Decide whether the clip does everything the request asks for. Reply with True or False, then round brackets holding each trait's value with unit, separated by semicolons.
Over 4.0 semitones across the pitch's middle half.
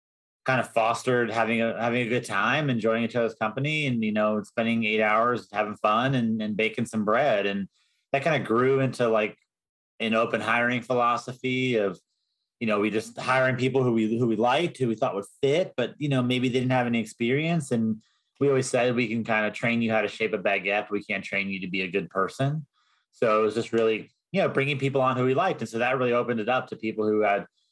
False (2.8 semitones)